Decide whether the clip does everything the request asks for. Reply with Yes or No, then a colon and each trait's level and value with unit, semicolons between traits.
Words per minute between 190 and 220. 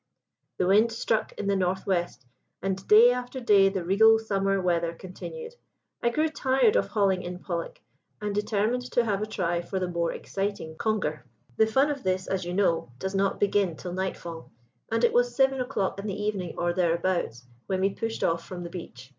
Yes: average, 200 wpm